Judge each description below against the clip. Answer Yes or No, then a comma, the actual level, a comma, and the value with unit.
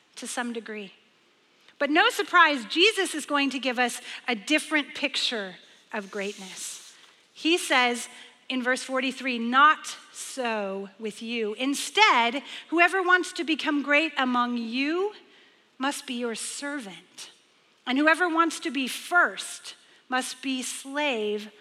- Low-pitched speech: No, very high, 265 Hz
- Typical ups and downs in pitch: Yes, average, 4.7 semitones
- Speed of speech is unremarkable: No, slow, 130 wpm